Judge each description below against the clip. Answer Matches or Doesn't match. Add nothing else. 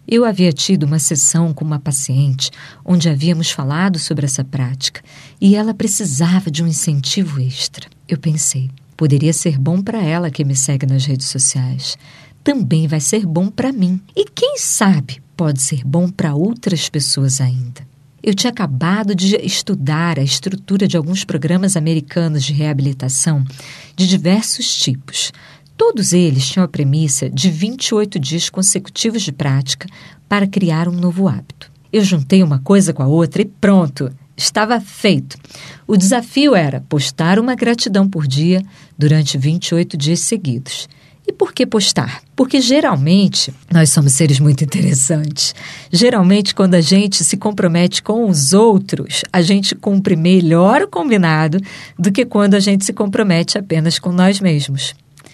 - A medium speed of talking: Matches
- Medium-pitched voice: Matches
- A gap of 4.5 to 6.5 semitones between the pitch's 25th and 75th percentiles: Matches